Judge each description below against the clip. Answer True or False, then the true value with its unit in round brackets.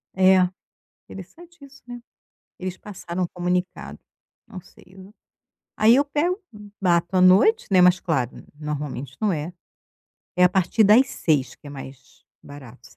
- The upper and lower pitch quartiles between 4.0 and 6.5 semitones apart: True (5.2 semitones)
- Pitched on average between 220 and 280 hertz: False (185 Hz)